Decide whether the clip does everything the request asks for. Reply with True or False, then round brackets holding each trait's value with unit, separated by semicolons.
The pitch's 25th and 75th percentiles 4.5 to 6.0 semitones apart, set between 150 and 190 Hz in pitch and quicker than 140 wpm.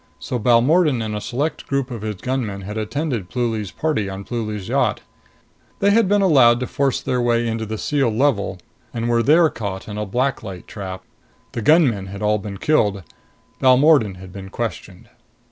False (5.0 semitones; 115 Hz; 180 wpm)